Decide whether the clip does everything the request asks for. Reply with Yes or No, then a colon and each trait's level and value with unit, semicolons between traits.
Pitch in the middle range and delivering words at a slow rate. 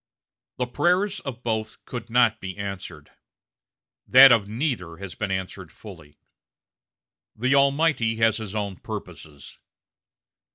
No: low, 110 Hz; slow, 120 wpm